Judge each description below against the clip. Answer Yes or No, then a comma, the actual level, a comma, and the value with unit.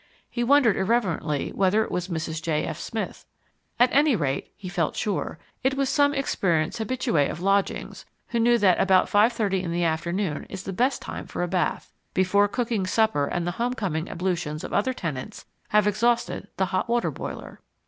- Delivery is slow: No, average, 185 wpm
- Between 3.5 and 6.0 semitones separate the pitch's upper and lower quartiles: Yes, average, 5.2 semitones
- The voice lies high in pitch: Yes, high, 195 Hz